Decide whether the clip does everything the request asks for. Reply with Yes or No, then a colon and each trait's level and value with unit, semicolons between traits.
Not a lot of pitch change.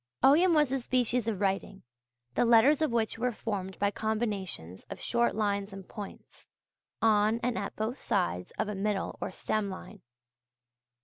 No: average, 3.3 semitones